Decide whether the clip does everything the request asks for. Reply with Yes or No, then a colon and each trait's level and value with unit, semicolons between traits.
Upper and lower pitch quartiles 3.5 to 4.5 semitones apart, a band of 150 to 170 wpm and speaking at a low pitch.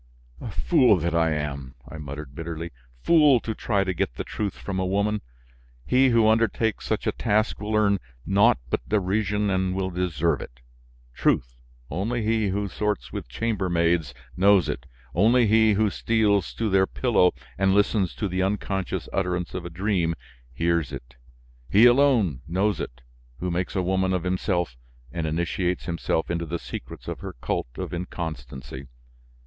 Yes: average, 4.0 semitones; average, 165 wpm; very low, 95 Hz